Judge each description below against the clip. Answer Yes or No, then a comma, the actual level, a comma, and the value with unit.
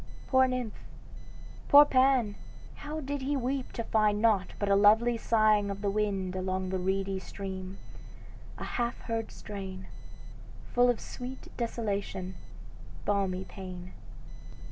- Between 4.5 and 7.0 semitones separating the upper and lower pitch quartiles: No, average, 4.0 semitones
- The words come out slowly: Yes, slow, 130 wpm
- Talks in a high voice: Yes, high, 210 Hz